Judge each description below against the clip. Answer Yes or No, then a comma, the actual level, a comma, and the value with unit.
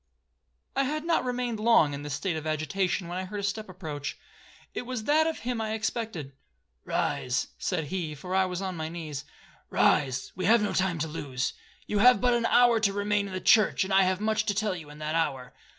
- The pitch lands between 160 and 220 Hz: Yes, high, 190 Hz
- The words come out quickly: Yes, fast, 215 wpm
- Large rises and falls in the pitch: Yes, wide, 5.7 semitones